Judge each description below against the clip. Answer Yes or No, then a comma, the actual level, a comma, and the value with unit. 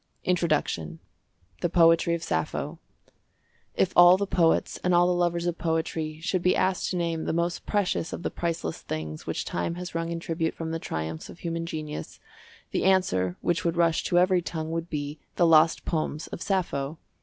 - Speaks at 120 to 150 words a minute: No, average, 185 wpm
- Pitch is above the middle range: No, medium, 165 Hz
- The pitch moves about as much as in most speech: No, narrow, 1.8 semitones